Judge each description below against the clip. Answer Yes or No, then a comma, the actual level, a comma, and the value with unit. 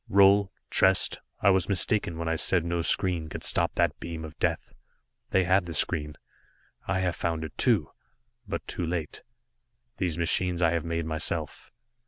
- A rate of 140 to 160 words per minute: No, average, 170 wpm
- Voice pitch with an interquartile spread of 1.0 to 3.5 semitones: Yes, narrow, 2.4 semitones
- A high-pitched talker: No, very low, 85 Hz